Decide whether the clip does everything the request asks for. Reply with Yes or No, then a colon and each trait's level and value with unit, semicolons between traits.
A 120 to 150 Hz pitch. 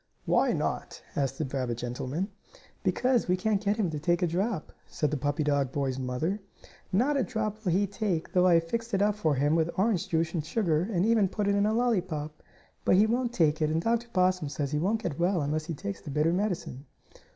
No: medium, 175 Hz